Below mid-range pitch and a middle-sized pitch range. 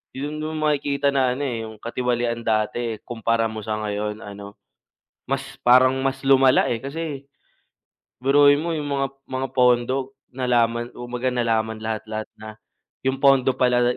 Yes: low, 125 Hz; average, 3.1 semitones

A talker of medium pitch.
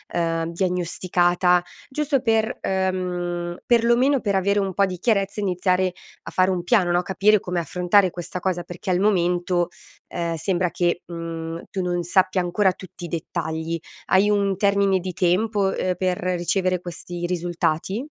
Yes: medium, 180 Hz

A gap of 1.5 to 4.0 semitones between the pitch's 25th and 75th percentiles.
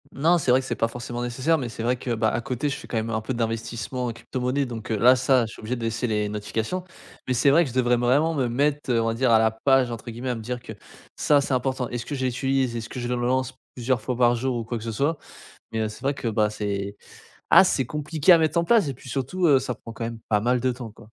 Yes: average, 2.7 semitones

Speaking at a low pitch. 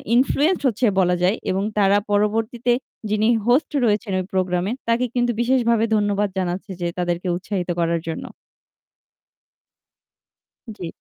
No: high, 205 Hz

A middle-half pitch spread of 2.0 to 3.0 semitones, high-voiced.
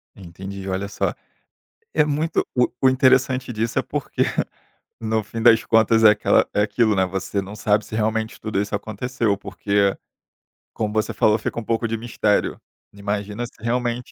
No: narrow, 2.4 semitones; low, 110 Hz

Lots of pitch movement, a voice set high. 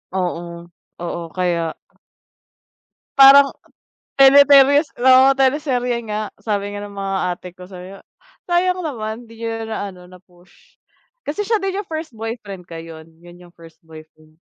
Yes: wide, 7.3 semitones; high, 215 Hz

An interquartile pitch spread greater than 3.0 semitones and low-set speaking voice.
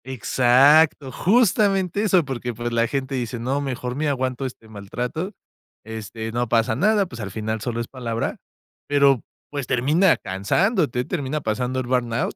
Yes: average, 3.8 semitones; low, 130 Hz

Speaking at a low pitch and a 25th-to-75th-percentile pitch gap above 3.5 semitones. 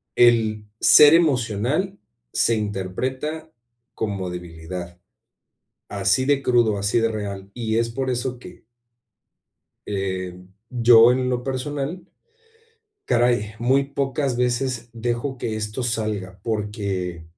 Yes: low, 115 Hz; average, 4.1 semitones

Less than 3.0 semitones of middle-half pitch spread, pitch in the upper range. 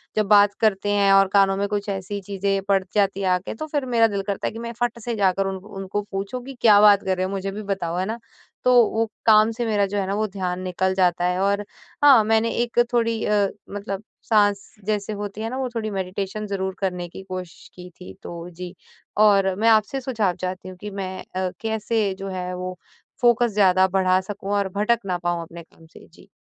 Yes: narrow, 2.4 semitones; high, 200 Hz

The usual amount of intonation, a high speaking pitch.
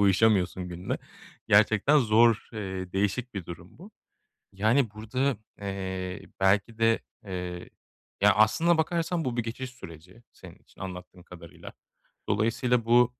No: average, 4.4 semitones; low, 105 Hz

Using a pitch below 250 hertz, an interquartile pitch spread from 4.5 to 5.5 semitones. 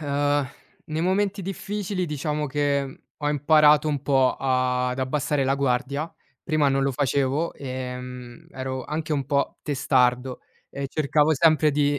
No: medium, 140 Hz; narrow, 2.5 semitones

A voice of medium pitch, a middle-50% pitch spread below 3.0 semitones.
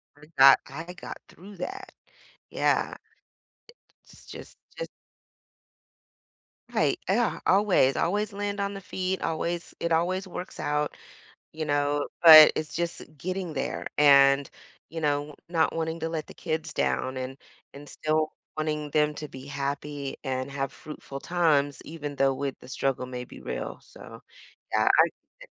No: medium, 150 Hz; average, 3.3 semitones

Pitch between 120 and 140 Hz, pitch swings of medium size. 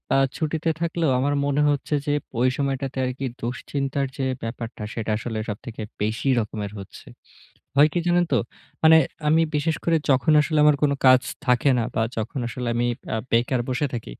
Yes: low, 135 Hz; average, 4.0 semitones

